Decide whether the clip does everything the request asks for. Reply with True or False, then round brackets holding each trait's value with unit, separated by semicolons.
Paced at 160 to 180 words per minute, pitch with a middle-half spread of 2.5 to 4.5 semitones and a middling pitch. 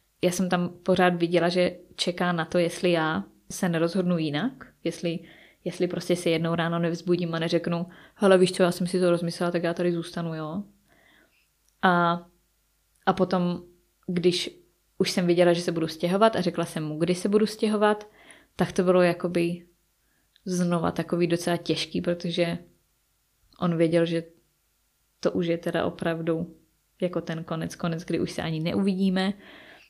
False (165 wpm; 1.3 semitones; 175 Hz)